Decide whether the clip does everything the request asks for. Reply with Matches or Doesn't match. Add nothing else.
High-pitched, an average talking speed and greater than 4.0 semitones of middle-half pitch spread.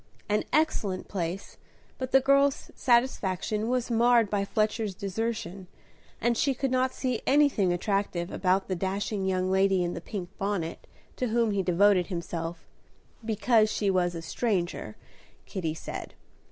Matches